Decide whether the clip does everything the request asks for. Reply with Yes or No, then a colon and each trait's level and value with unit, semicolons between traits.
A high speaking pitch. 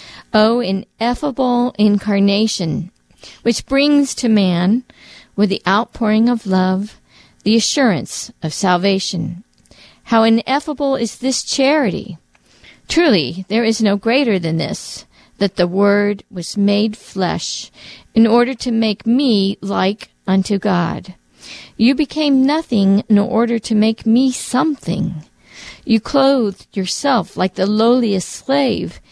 Yes: high, 220 Hz